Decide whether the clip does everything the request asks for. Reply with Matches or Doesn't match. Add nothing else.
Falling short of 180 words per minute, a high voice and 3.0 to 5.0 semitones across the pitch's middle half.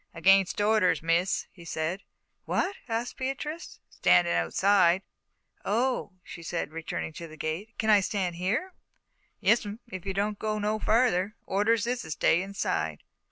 Matches